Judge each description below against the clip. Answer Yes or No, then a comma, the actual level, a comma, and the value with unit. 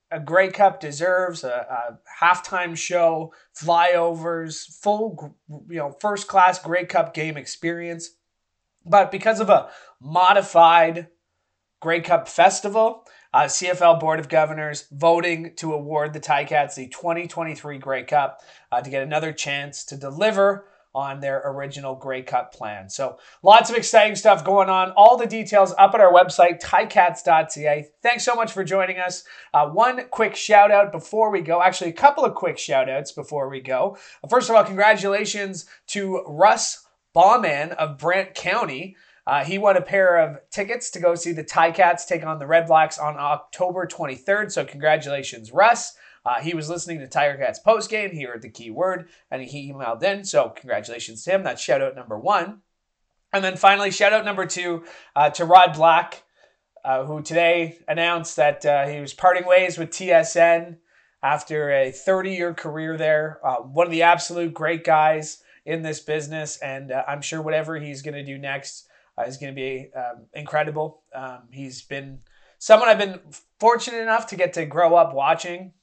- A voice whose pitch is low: No, medium, 165 Hz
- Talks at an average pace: Yes, average, 175 wpm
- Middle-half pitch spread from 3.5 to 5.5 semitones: Yes, average, 4.1 semitones